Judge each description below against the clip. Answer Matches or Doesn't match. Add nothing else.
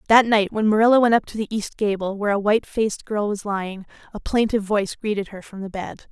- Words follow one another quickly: Matches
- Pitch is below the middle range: Doesn't match